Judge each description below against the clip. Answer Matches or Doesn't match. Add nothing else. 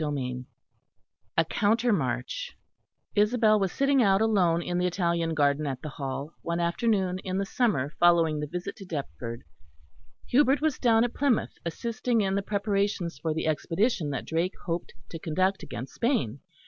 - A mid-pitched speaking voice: Matches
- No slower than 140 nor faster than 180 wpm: Matches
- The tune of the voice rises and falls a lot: Matches